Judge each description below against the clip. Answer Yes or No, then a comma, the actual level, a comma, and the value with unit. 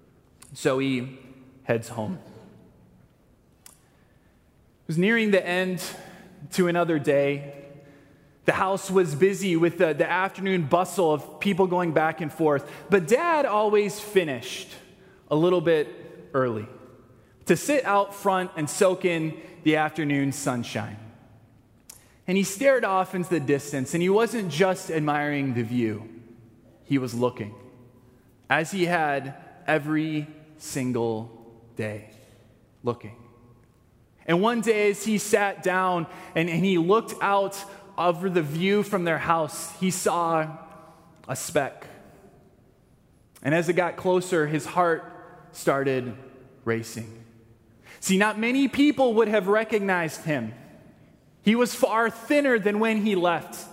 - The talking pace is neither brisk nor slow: No, slow, 130 wpm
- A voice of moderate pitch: Yes, medium, 165 Hz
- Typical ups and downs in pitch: No, wide, 6.8 semitones